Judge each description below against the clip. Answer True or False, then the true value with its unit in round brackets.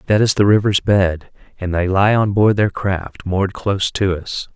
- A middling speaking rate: False (210 wpm)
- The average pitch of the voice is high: False (100 Hz)